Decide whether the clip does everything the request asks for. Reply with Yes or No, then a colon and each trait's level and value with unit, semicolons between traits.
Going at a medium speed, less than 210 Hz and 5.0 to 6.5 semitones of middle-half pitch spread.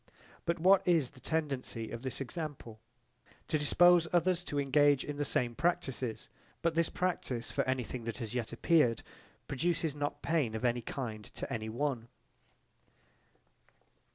Yes: average, 150 wpm; medium, 140 Hz; wide, 5.4 semitones